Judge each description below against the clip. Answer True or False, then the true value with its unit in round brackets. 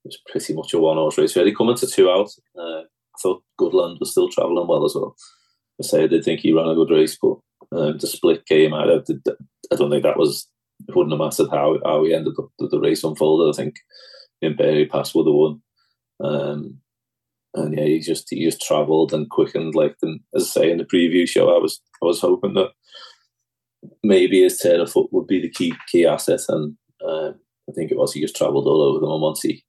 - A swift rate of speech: True (240 wpm)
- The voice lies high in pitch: True (385 Hz)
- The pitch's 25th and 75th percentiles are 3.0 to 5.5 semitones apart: False (2.6 semitones)